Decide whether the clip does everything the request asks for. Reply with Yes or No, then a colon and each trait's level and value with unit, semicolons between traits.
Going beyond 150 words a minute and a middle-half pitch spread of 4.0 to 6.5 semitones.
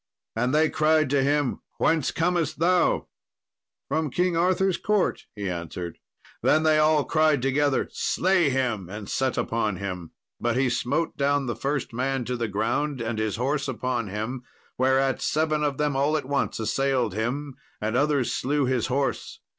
Yes: average, 165 wpm; average, 4.3 semitones